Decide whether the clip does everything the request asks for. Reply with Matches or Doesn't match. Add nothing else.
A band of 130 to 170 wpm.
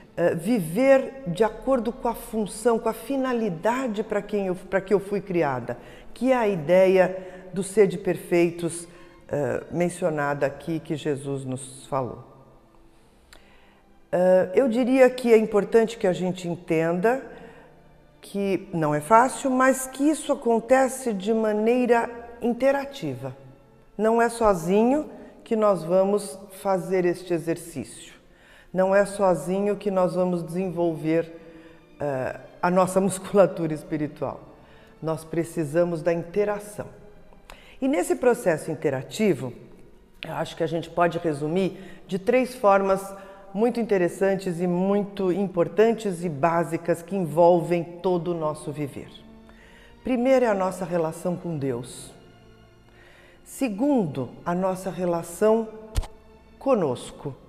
Doesn't match